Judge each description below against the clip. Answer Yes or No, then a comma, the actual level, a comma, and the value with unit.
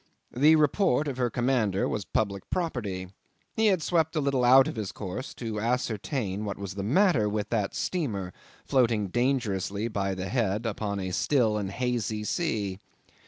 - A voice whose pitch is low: Yes, low, 115 Hz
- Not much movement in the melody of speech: No, average, 5.0 semitones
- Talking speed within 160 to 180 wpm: Yes, average, 165 wpm